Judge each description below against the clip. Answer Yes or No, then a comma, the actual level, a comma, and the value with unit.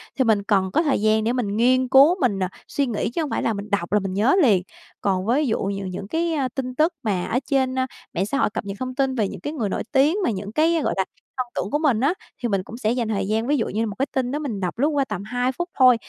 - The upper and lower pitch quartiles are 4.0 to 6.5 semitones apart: Yes, average, 5.1 semitones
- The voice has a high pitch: Yes, high, 240 Hz